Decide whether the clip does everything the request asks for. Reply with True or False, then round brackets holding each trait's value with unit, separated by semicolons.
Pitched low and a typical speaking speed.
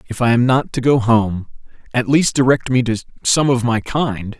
False (120 Hz; 220 wpm)